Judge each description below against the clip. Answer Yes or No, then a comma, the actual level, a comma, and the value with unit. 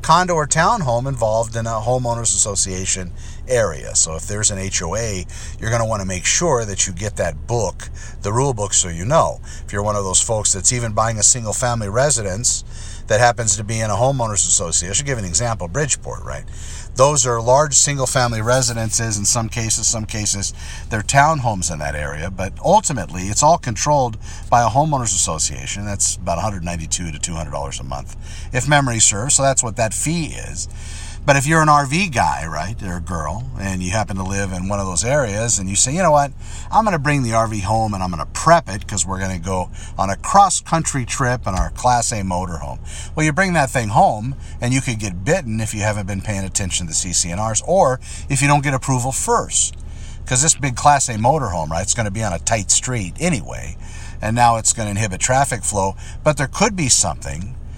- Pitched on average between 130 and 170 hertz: No, low, 105 Hz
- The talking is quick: Yes, fast, 220 wpm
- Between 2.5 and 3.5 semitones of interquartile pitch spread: No, average, 5.2 semitones